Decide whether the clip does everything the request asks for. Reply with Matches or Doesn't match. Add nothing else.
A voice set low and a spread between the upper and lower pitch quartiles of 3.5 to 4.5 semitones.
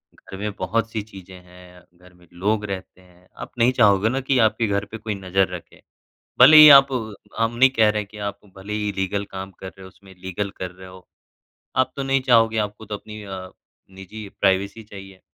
Doesn't match